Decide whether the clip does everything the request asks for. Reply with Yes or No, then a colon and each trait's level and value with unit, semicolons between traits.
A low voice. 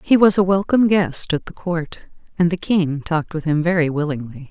No: medium, 170 Hz